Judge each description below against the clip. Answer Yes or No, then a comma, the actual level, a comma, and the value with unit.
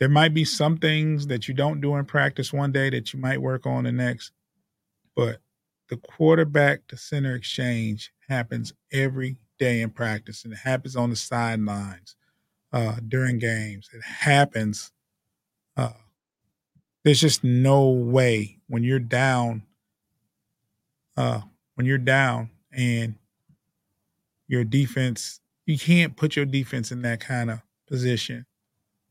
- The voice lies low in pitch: Yes, low, 125 Hz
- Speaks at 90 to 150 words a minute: Yes, slow, 135 wpm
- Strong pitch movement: No, average, 3.3 semitones